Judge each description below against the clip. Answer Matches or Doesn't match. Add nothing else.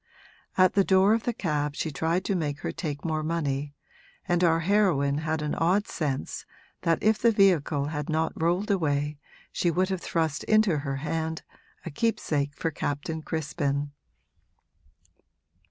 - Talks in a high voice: Doesn't match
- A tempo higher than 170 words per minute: Doesn't match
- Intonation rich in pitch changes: Doesn't match